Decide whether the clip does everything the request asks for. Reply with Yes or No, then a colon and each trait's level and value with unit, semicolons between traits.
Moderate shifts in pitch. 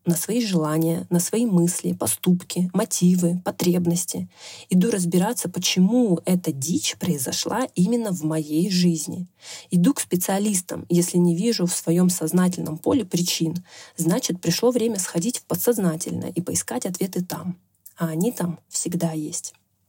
No: narrow, 2.0 semitones